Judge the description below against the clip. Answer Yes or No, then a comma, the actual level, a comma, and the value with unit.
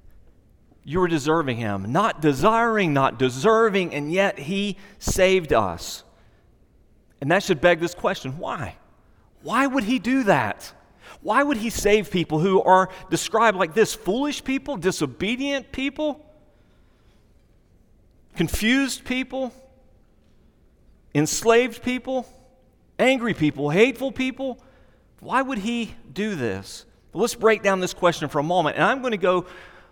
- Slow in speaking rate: Yes, slow, 130 wpm